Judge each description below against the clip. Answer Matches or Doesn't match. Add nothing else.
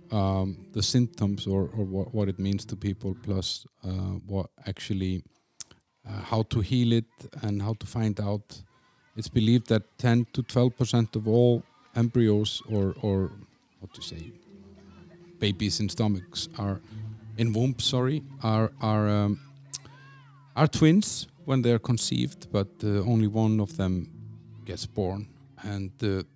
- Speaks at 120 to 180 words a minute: Matches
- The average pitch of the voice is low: Matches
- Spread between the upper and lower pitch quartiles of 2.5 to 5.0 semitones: Matches